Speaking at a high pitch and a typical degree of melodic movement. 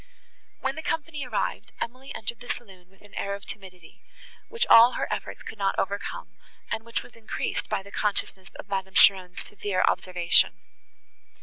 Yes: high, 200 Hz; average, 3.6 semitones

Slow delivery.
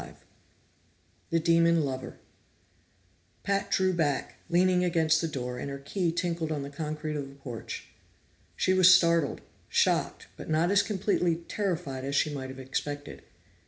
No: average, 155 wpm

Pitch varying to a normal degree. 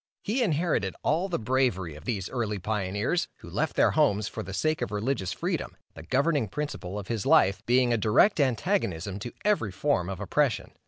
No: wide, 7.0 semitones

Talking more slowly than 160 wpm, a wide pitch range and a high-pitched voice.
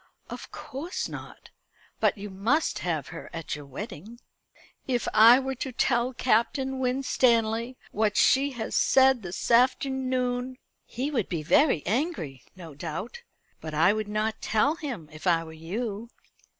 Yes: average, 150 wpm; wide, 6.1 semitones; high, 230 Hz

